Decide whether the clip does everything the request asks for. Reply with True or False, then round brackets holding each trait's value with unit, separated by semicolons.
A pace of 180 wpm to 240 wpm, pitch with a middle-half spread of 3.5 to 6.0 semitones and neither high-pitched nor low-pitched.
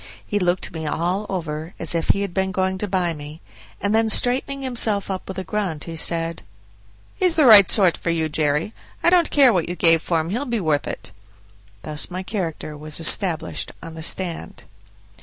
True (200 wpm; 4.2 semitones; 180 Hz)